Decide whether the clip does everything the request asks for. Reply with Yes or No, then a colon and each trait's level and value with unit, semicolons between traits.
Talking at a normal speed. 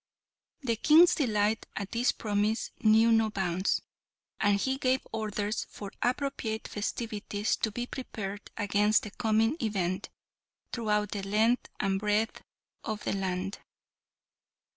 No: slow, 125 wpm